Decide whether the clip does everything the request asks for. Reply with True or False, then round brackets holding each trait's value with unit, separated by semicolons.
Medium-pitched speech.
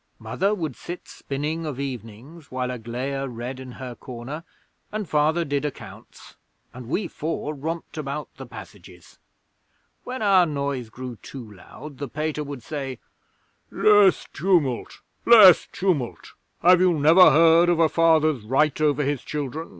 True (145 Hz)